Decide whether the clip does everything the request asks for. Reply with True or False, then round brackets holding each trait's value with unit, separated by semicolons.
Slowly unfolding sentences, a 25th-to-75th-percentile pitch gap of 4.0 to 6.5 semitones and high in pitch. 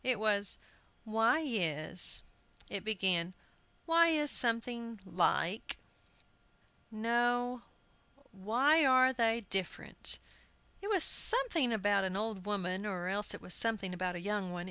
True (130 wpm; 4.4 semitones; 215 Hz)